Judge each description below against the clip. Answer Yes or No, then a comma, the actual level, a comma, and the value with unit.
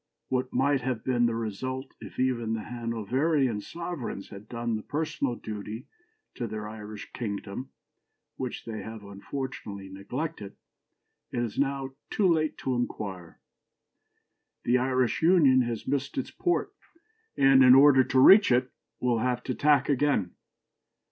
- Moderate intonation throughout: Yes, average, 3.6 semitones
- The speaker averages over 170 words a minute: No, average, 140 wpm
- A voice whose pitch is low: Yes, low, 125 Hz